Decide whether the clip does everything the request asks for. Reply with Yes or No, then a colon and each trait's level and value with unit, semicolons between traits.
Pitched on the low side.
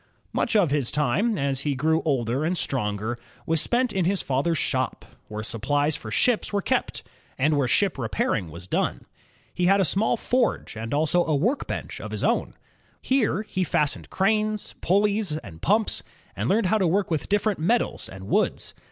No: medium, 160 Hz